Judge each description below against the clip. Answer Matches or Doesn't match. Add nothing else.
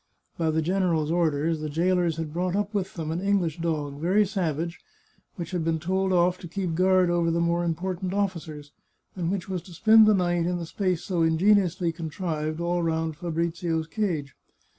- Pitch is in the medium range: Matches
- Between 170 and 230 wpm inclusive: Matches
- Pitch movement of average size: Doesn't match